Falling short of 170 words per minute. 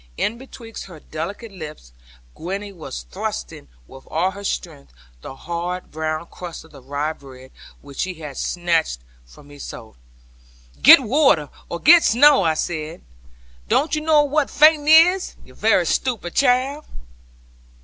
Yes: average, 150 wpm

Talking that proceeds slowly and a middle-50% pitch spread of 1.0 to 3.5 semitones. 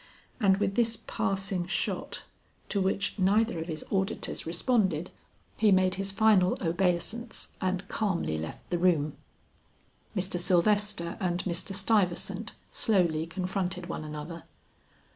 Yes: slow, 125 wpm; narrow, 2.6 semitones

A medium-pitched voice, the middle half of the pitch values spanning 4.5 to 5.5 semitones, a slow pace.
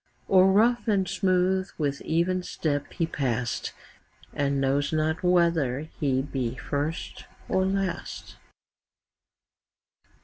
Yes: medium, 160 Hz; average, 4.8 semitones; slow, 110 wpm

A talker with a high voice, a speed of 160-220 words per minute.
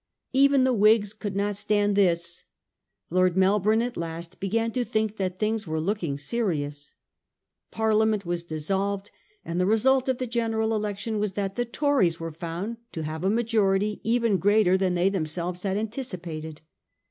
Yes: high, 200 Hz; average, 165 wpm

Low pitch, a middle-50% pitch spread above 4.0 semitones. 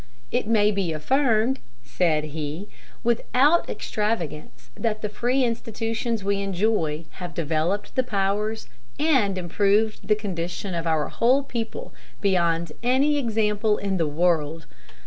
No: high, 205 Hz; average, 5.1 semitones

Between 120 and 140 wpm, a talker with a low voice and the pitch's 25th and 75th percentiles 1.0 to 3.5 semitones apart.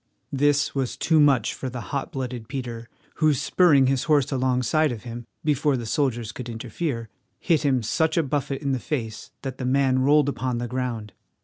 No: average, 190 wpm; low, 130 Hz; average, 3.2 semitones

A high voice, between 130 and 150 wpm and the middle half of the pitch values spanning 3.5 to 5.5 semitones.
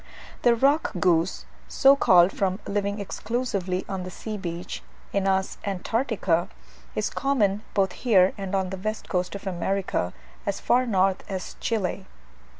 No: high, 195 Hz; average, 145 wpm; average, 2.7 semitones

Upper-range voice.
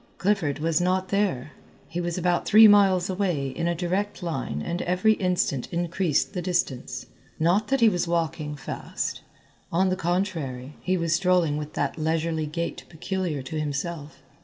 No: medium, 170 Hz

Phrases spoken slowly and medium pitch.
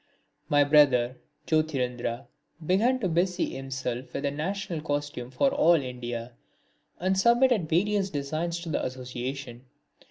Yes: slow, 125 wpm; medium, 145 Hz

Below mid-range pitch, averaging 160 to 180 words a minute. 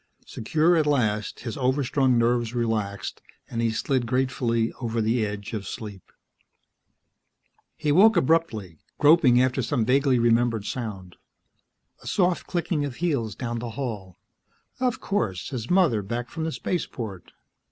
No: low, 120 Hz; average, 140 wpm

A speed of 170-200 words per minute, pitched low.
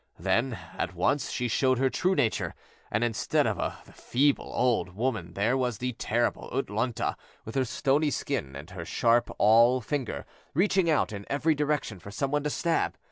Yes: average, 180 wpm; low, 125 Hz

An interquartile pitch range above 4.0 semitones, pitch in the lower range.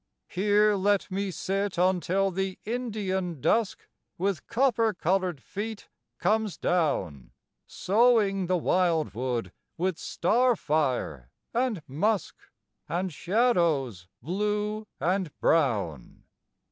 No: average, 4.4 semitones; high, 190 Hz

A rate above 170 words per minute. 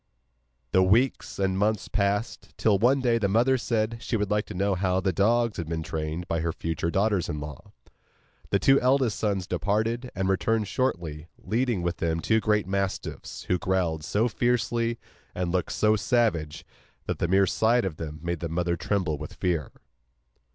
Yes: average, 180 wpm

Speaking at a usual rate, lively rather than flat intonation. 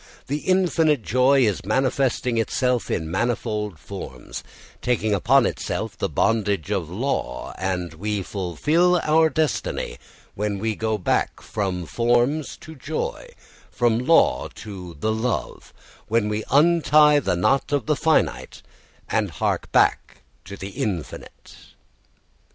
No: slow, 130 wpm; wide, 6.0 semitones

